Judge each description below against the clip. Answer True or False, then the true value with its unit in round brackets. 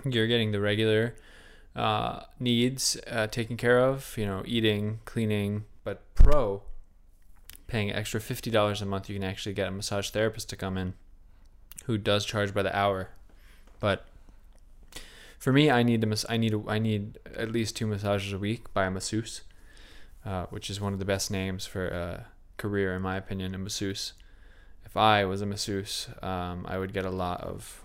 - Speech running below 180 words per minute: False (185 wpm)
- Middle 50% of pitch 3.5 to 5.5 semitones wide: False (2.7 semitones)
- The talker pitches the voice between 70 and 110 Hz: True (100 Hz)